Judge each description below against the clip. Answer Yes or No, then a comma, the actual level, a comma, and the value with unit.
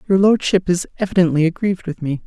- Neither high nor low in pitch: Yes, medium, 180 Hz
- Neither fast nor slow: Yes, average, 185 wpm